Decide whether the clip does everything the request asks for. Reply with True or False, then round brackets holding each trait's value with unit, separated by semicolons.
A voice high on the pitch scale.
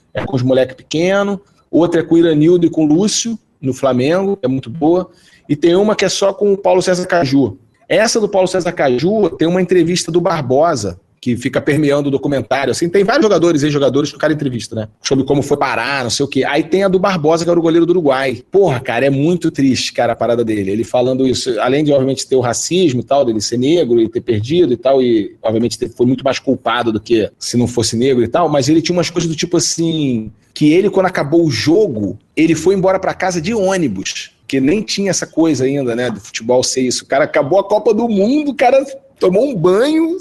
False (155 Hz)